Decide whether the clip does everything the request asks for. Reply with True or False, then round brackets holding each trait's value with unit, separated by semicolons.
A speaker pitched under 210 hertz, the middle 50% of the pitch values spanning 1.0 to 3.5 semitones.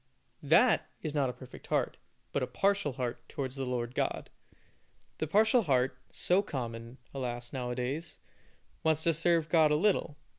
False (140 Hz; 4.8 semitones)